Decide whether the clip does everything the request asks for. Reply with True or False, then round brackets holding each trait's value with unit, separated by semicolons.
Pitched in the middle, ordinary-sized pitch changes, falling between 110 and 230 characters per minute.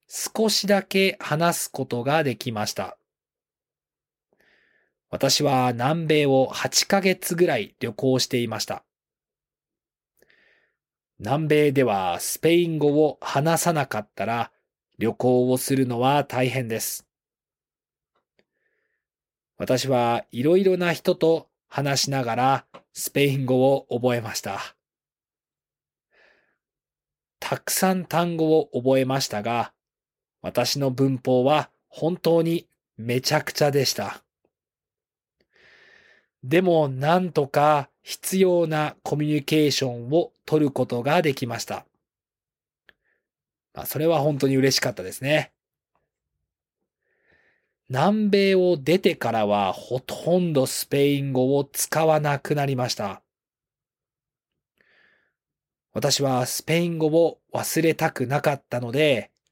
True (145 Hz; 4.2 semitones; 205 characters per minute)